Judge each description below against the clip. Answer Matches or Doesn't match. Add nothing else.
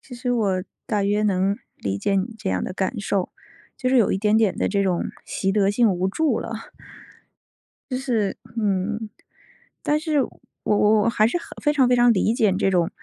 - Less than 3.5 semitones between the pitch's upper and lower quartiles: Doesn't match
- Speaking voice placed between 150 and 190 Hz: Doesn't match